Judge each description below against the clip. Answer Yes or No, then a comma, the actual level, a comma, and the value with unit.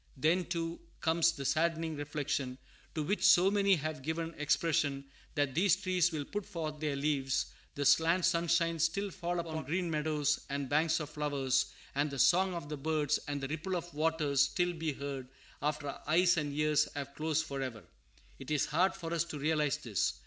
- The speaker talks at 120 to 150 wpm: No, average, 185 wpm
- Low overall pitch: No, medium, 155 Hz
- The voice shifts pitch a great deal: No, average, 2.7 semitones